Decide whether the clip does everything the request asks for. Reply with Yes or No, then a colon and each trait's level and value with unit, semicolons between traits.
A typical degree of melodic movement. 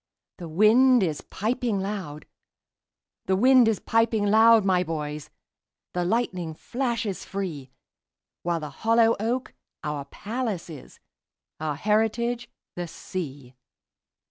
No: wide, 6.0 semitones